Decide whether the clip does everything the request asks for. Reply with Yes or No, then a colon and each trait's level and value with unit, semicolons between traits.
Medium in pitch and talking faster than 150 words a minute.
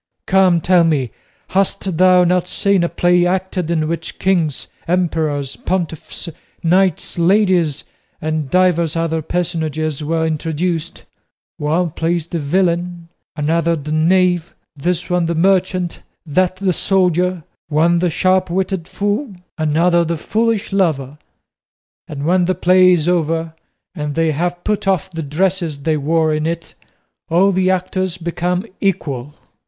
No: medium, 170 Hz; slow, 135 wpm